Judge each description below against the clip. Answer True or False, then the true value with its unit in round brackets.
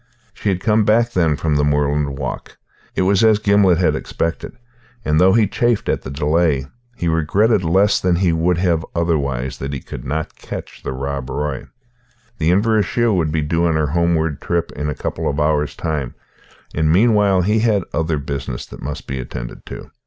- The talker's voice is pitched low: True (80 Hz)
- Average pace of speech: True (190 wpm)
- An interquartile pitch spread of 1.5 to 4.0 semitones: False (4.6 semitones)